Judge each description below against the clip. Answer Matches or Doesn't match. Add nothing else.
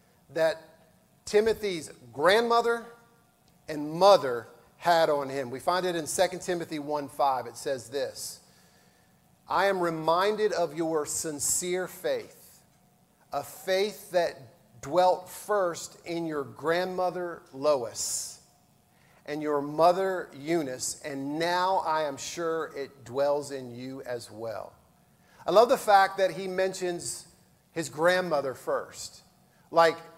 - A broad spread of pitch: Doesn't match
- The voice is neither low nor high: Matches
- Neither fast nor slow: Doesn't match